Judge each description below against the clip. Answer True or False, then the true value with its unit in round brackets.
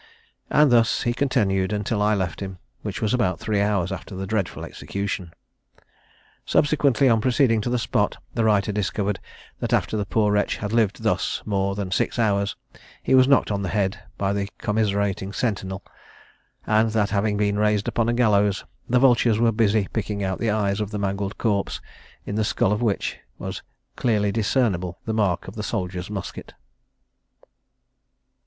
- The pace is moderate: True (175 wpm)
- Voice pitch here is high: False (105 Hz)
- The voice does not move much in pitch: True (2.2 semitones)